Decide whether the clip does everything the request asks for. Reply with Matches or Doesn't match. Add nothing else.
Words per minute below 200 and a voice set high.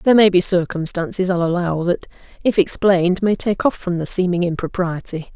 Doesn't match